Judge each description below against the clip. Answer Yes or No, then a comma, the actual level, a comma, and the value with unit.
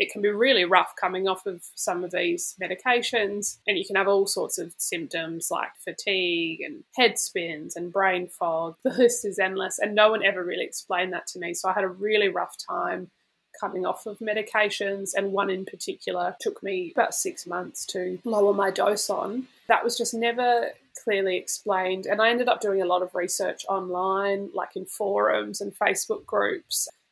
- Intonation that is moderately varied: Yes, average, 4.1 semitones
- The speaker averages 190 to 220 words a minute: Yes, average, 195 wpm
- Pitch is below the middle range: No, high, 200 Hz